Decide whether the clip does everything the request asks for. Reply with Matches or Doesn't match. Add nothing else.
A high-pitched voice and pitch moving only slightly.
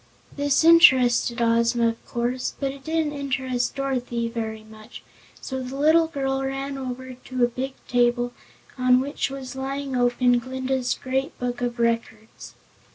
Matches